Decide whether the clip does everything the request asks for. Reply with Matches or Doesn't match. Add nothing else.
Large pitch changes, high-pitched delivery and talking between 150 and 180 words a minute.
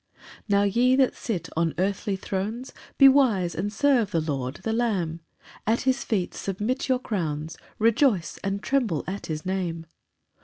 Matches